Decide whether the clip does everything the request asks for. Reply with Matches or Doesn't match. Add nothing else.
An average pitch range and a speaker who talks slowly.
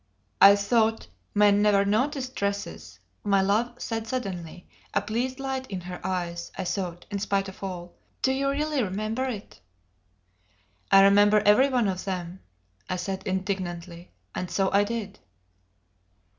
Doesn't match